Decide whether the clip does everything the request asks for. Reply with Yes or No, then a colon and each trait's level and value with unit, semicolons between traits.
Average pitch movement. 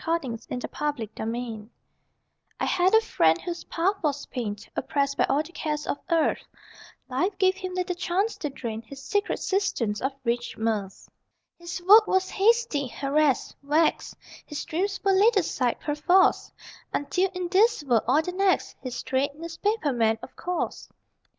No: wide, 6.4 semitones